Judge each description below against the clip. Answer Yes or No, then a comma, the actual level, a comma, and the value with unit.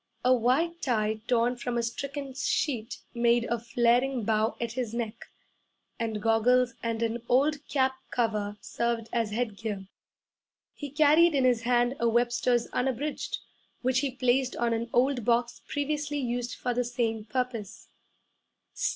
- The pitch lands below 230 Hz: No, high, 240 Hz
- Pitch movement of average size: No, narrow, 2.2 semitones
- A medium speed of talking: Yes, average, 145 wpm